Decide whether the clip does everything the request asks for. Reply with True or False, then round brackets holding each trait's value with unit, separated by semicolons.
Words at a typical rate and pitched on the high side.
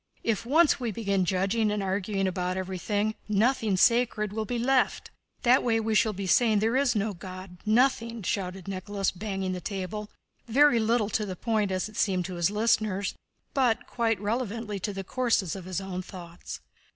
True (175 wpm; 210 Hz)